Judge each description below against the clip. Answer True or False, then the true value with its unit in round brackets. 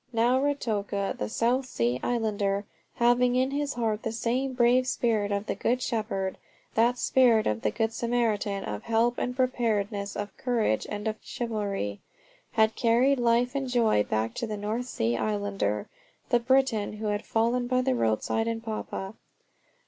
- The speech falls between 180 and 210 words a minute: False (165 wpm)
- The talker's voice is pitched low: False (225 Hz)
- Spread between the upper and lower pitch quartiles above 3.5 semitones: False (3.2 semitones)